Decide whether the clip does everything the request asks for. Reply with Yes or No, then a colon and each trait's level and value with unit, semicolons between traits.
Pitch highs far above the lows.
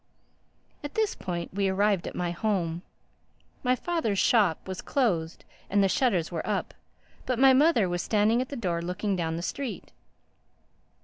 Yes: wide, 6.1 semitones